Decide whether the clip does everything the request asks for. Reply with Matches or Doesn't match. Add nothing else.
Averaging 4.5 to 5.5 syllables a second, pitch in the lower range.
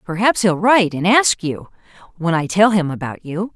Doesn't match